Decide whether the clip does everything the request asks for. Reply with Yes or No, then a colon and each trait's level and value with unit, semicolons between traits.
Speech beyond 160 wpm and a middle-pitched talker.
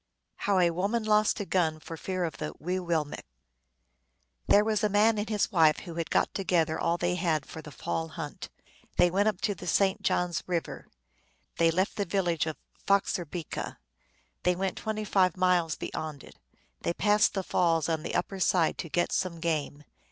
Yes: average, 195 wpm; medium, 180 Hz